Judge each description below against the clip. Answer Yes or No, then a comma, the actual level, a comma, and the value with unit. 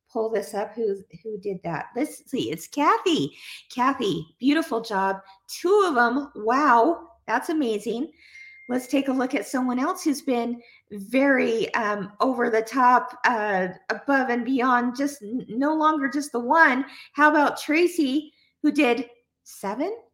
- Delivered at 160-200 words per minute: No, average, 150 wpm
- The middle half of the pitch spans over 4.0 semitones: Yes, average, 4.7 semitones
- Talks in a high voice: Yes, very high, 250 Hz